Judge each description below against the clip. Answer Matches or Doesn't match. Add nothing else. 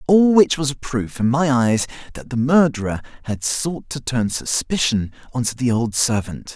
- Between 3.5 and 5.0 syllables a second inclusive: Matches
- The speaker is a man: Matches